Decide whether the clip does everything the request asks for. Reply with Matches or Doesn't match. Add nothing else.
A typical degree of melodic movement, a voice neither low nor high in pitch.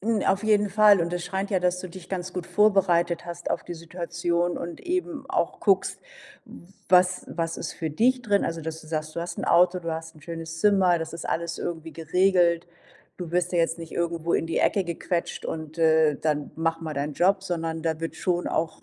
Doesn't match